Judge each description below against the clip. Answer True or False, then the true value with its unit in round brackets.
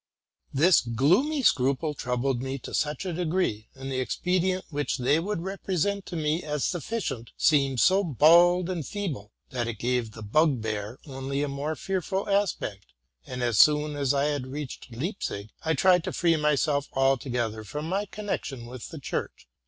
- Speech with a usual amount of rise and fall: False (5.7 semitones)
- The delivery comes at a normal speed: True (170 wpm)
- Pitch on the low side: False (145 Hz)